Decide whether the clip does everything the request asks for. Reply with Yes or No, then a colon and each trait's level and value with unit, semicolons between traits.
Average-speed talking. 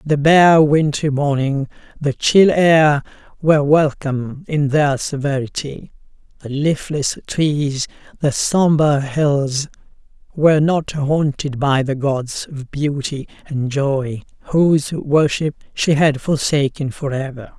No: slow, 120 wpm